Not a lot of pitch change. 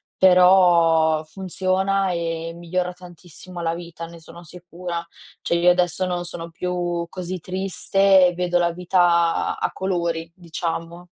Yes: narrow, 1.3 semitones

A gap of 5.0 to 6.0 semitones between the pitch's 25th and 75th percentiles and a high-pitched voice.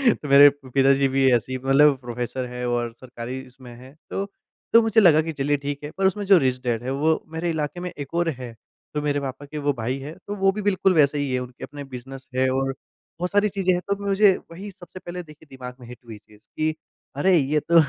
No: wide, 5.4 semitones; medium, 145 Hz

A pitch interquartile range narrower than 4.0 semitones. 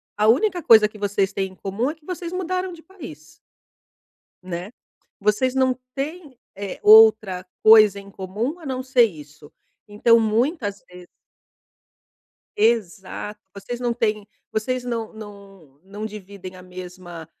No: average, 4.8 semitones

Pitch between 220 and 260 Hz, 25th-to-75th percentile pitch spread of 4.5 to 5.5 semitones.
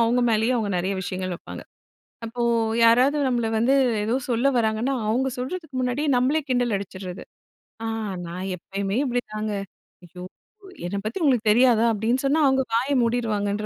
No: high, 230 Hz; average, 3.7 semitones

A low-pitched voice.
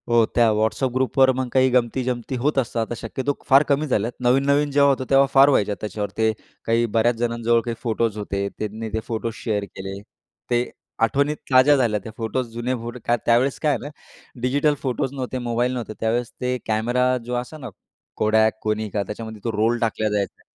Yes: low, 120 Hz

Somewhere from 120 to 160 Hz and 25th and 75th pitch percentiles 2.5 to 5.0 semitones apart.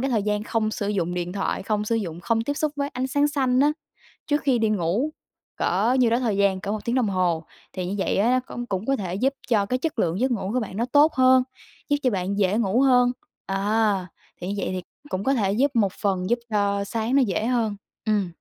No: high, 215 Hz; average, 4.5 semitones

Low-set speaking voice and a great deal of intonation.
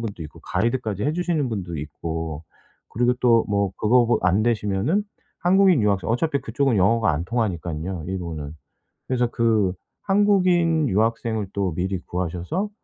Yes: low, 110 Hz; wide, 6.2 semitones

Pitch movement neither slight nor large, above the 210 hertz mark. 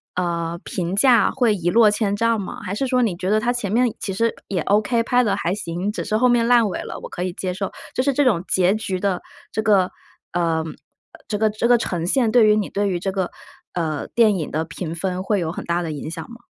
No: average, 4.5 semitones; high, 200 Hz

